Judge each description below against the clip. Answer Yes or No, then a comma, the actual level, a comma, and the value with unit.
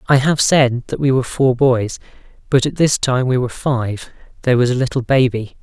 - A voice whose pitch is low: Yes, low, 130 Hz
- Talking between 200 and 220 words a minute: Yes, fast, 205 wpm